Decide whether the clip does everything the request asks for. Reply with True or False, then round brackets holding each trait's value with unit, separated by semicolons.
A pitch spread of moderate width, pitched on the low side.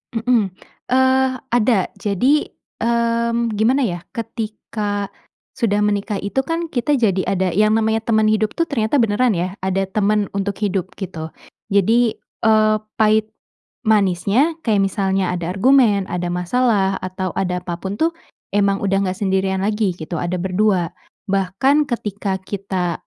False (3.3 semitones; 205 Hz)